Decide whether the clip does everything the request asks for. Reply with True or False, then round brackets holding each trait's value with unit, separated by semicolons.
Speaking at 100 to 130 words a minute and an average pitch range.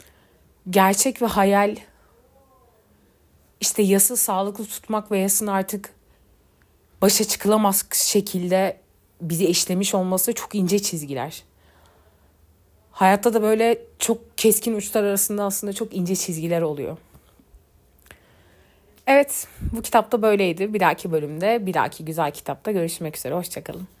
True (110 wpm; 4.2 semitones)